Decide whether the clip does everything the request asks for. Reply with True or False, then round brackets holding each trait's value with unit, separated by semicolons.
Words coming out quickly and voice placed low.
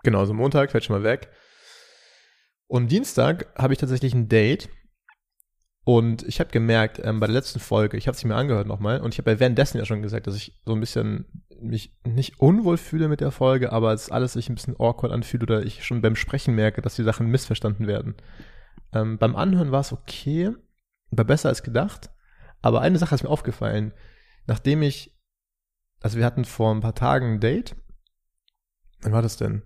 True (210 wpm; 115 Hz)